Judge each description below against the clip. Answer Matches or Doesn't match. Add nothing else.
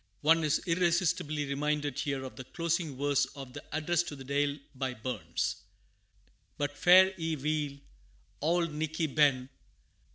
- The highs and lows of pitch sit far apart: Doesn't match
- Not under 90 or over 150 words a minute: Matches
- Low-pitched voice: Doesn't match